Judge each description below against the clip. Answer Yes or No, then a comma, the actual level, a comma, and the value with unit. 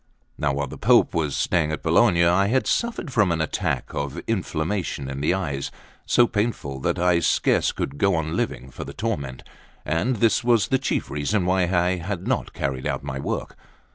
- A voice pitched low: Yes, very low, 85 Hz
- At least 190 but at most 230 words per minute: Yes, average, 195 wpm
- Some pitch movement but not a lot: No, wide, 6.0 semitones